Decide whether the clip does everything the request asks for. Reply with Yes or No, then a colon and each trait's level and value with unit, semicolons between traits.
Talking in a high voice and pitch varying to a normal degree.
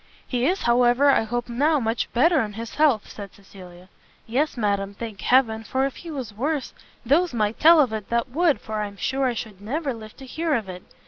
Yes: high, 240 Hz; average, 4.6 semitones